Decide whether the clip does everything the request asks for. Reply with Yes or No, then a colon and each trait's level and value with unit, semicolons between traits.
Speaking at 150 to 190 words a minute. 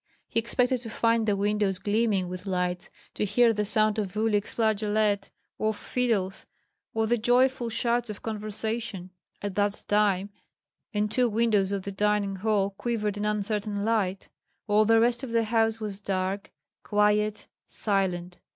Yes: average, 155 wpm